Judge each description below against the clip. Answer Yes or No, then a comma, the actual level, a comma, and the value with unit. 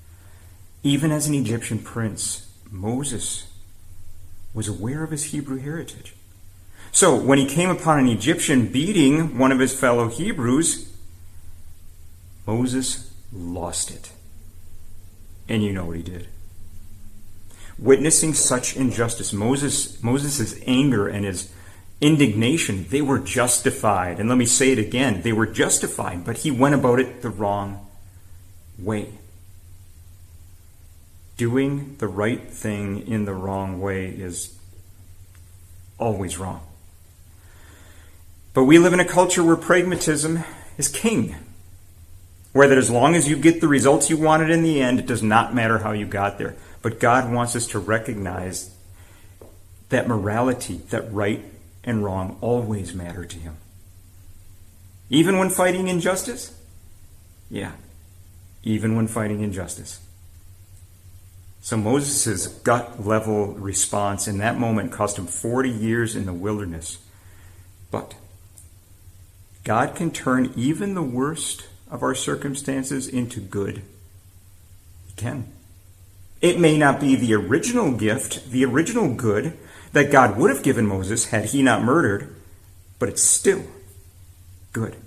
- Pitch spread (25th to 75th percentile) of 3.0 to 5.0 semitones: No, wide, 5.5 semitones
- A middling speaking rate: No, slow, 130 wpm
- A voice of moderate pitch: No, low, 100 Hz